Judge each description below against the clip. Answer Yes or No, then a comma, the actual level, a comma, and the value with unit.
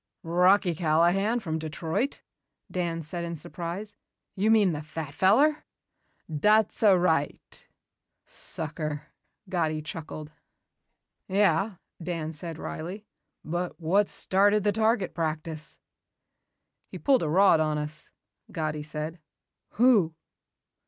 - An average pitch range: Yes, average, 4.2 semitones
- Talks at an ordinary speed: No, slow, 105 wpm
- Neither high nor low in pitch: Yes, medium, 170 Hz